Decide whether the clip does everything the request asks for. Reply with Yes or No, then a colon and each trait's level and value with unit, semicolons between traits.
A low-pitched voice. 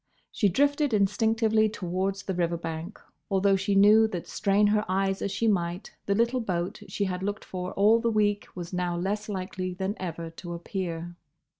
No: high, 195 Hz